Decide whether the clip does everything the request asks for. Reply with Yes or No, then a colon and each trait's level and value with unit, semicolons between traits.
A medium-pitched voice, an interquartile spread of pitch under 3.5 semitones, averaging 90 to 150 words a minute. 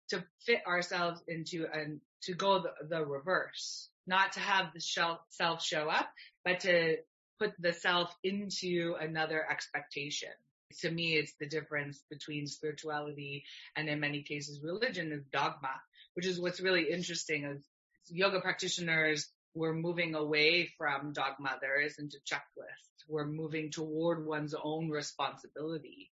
Yes: medium, 160 Hz; average, 2.8 semitones; average, 140 wpm